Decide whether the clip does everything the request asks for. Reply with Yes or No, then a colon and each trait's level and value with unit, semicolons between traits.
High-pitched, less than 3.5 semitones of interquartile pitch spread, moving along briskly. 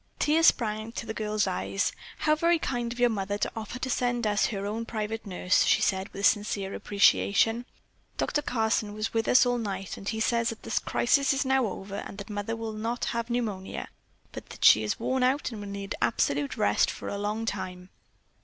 Yes: high, 220 Hz; average, 3.1 semitones; fast, 210 wpm